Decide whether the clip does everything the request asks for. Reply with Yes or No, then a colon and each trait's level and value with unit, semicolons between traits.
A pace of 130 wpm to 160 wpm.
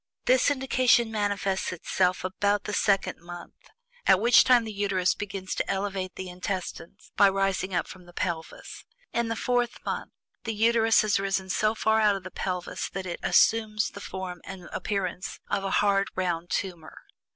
No: average, 175 wpm